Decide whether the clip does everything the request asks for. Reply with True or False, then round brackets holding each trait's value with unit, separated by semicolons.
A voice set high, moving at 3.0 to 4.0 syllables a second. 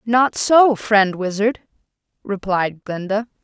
True (210 Hz; 3.4 syllables/s)